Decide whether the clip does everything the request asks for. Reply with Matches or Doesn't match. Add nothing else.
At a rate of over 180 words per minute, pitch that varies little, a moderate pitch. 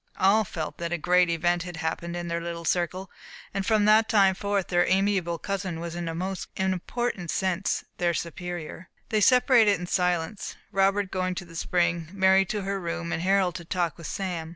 Matches